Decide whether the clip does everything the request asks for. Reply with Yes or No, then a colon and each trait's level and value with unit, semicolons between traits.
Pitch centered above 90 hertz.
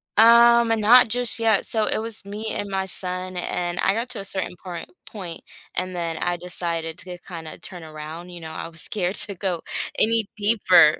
Yes: medium, 185 Hz